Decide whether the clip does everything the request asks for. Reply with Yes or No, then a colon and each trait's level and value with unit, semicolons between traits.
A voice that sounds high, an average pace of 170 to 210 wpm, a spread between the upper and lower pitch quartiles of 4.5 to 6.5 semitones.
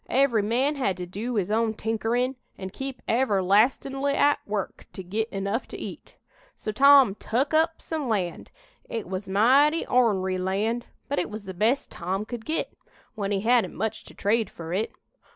Yes: high, 220 Hz; average, 175 wpm; average, 4.8 semitones